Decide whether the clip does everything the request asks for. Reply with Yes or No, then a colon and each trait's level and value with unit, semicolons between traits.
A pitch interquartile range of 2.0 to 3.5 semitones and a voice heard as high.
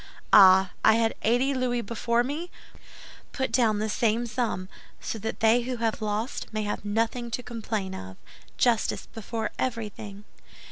Yes: narrow, 2.4 semitones; high, 225 Hz